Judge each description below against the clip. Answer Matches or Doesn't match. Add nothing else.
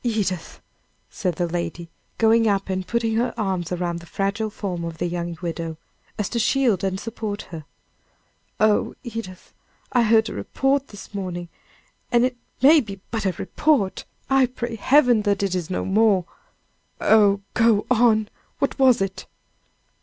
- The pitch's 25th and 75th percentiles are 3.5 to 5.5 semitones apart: Matches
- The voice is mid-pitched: Doesn't match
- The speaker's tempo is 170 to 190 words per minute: Doesn't match